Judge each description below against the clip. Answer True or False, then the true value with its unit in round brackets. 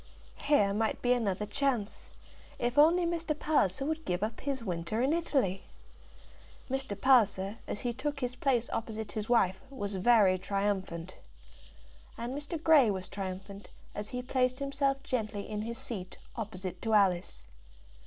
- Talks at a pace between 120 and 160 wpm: True (150 wpm)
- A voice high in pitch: True (225 Hz)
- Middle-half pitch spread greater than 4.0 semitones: True (5.3 semitones)